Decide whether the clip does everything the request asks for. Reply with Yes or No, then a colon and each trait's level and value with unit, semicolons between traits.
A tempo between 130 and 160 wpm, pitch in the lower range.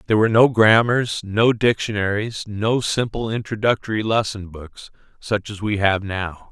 Yes: average, 145 wpm; low, 105 Hz